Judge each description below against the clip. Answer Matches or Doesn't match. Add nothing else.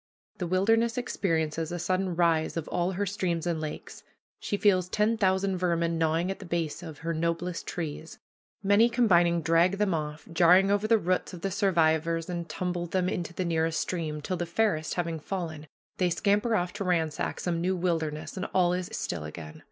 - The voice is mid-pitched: Matches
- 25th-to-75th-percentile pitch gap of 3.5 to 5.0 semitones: Doesn't match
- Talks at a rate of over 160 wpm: Matches